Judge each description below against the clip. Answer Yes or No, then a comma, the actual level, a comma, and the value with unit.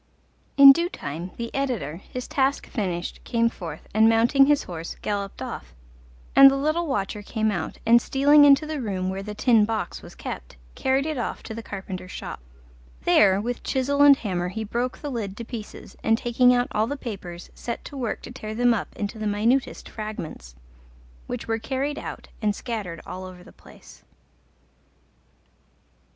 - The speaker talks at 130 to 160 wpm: No, average, 180 wpm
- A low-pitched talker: No, high, 225 Hz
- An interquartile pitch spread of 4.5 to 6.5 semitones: Yes, average, 5.1 semitones